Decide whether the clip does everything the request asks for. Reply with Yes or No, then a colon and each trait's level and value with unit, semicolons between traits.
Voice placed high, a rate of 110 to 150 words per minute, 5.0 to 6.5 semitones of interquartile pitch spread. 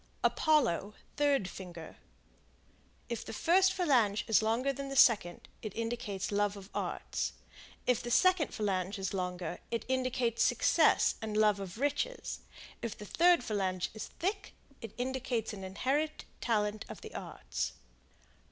Yes: high, 225 Hz; average, 145 wpm; average, 5.3 semitones